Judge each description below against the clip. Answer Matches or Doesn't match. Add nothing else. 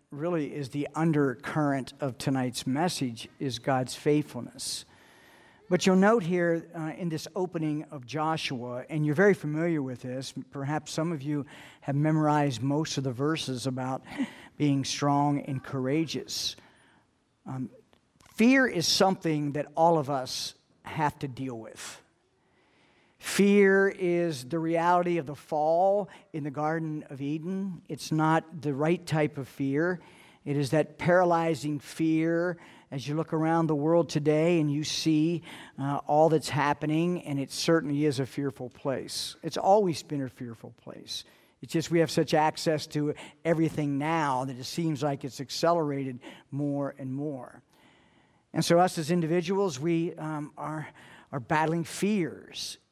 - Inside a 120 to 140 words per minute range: Doesn't match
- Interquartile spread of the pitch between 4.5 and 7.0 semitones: Doesn't match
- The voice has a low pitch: Doesn't match